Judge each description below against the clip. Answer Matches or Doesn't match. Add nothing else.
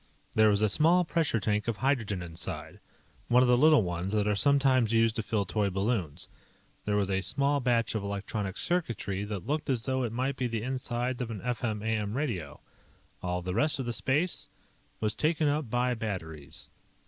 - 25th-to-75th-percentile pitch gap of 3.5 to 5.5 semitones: Matches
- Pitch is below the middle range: Matches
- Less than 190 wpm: Doesn't match